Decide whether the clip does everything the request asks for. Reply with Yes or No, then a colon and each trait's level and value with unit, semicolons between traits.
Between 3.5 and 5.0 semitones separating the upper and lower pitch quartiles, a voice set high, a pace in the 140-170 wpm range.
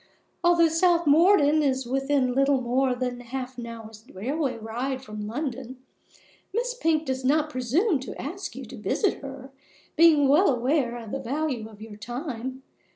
Yes: average, 4.2 semitones; very high, 265 Hz; average, 160 wpm